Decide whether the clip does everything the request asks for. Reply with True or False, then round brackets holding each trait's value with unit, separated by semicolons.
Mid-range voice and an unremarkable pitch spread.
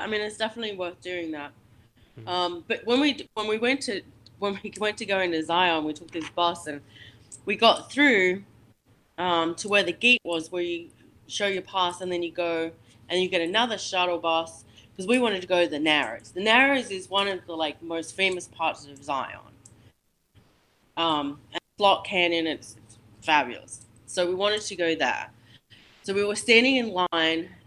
True (175 Hz; 4.9 semitones)